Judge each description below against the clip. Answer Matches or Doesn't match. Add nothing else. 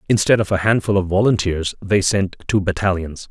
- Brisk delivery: Doesn't match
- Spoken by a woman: Doesn't match